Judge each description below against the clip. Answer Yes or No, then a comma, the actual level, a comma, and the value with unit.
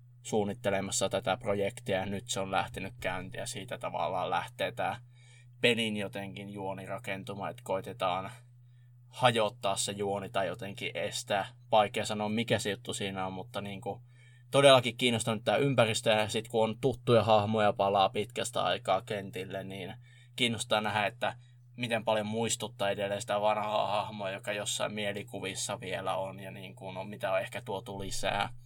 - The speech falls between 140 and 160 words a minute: Yes, fast, 155 wpm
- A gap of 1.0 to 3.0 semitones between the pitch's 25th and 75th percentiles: No, average, 3.5 semitones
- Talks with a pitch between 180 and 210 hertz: No, low, 105 Hz